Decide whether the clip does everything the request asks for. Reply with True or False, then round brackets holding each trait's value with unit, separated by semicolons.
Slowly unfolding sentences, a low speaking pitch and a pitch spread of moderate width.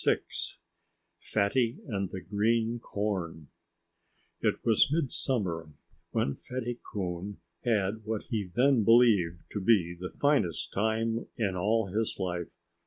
True (125 wpm; 105 Hz; 3.8 semitones)